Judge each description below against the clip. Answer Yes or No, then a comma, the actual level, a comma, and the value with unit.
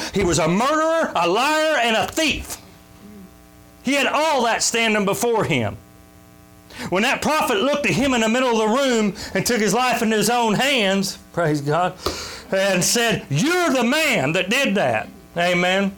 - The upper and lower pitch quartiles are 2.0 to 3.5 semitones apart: No, average, 5.3 semitones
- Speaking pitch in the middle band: No, high, 220 Hz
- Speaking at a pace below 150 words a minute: No, average, 175 wpm